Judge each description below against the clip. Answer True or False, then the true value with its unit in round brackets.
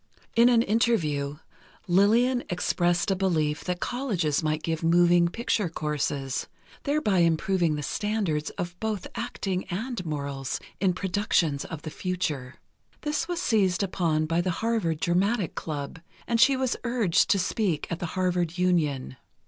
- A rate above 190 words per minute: False (145 wpm)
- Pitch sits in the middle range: True (180 Hz)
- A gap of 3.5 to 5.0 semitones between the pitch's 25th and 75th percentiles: False (5.5 semitones)